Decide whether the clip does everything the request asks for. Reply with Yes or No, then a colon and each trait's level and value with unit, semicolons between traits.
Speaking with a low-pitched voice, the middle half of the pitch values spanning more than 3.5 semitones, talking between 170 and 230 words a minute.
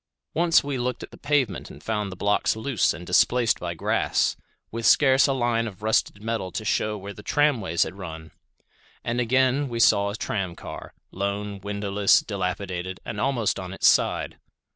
Yes: low, 105 Hz; average, 4.1 semitones; average, 180 wpm